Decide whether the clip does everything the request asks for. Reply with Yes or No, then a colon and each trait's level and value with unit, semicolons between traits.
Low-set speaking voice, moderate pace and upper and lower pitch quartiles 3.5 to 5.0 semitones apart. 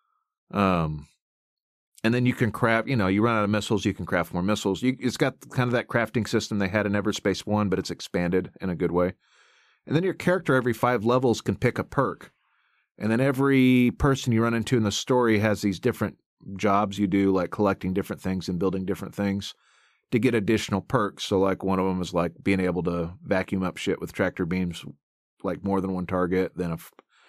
No: low, 100 Hz; fast, 220 wpm; average, 4.1 semitones